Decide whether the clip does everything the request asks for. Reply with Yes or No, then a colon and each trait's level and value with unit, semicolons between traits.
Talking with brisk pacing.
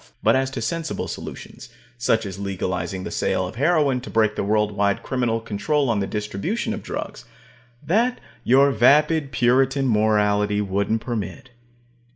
No: average, 155 wpm